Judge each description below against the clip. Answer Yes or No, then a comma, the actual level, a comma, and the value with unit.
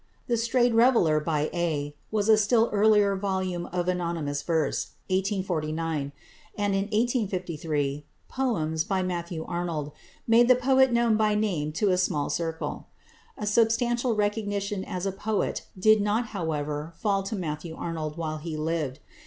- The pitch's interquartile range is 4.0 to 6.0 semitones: Yes, average, 5.1 semitones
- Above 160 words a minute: No, average, 145 wpm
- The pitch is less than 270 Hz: Yes, medium, 185 Hz